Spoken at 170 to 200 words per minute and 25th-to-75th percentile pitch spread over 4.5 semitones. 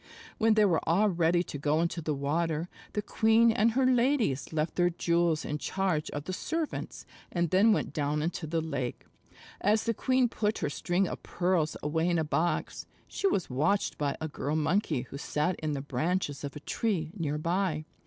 Yes: average, 195 wpm; average, 5.0 semitones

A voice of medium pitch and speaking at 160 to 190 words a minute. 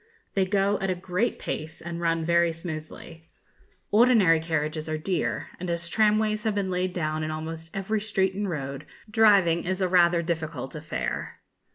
Yes: medium, 170 Hz; average, 170 wpm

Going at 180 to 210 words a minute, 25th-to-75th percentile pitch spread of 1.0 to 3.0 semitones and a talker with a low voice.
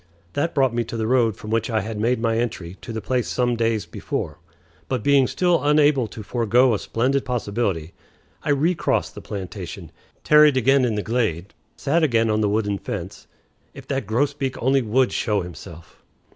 No: average, 185 wpm; average, 3.9 semitones; low, 115 Hz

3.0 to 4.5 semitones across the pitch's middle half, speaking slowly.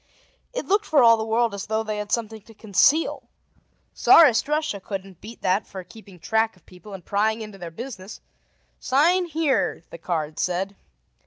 No: average, 4.0 semitones; average, 175 wpm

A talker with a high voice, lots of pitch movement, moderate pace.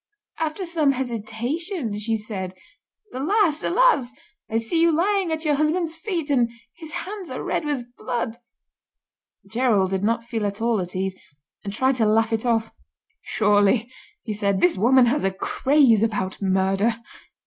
Yes: high, 235 Hz; wide, 6.6 semitones; average, 160 wpm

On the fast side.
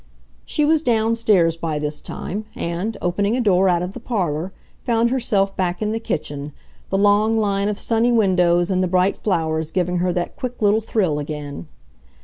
No: average, 180 wpm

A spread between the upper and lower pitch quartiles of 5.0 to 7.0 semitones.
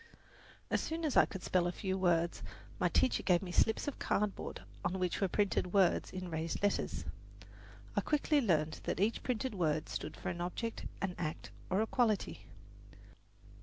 No: average, 3.8 semitones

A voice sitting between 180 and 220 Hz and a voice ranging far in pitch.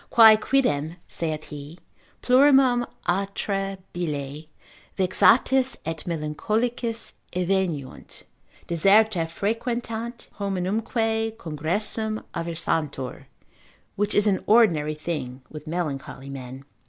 Yes: medium, 185 Hz; wide, 6.4 semitones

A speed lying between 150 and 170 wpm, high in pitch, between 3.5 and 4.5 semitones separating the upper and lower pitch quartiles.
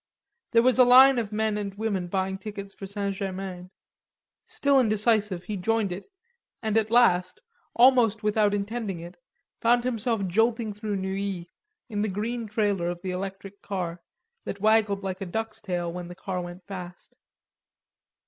No: average, 160 wpm; high, 200 Hz; average, 2.9 semitones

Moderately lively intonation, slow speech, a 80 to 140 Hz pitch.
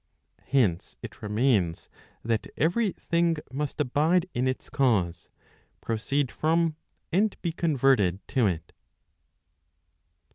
No: wide, 6.9 semitones; slow, 105 wpm; low, 135 Hz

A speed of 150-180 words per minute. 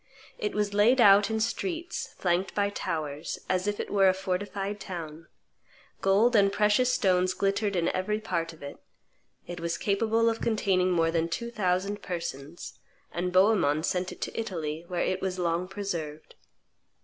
Yes: average, 165 wpm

